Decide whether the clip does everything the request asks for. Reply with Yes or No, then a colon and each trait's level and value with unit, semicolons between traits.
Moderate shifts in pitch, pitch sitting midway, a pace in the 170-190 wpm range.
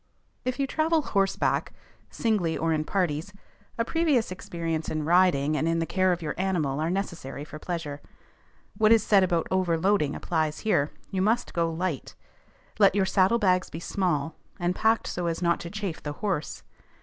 Yes: average, 3.8 semitones; medium, 180 Hz; average, 175 wpm